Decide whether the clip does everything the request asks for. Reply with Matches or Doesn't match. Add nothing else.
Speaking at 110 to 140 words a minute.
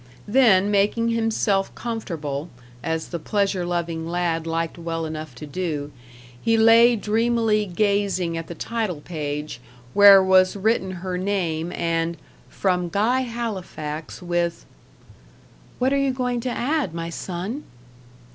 Matches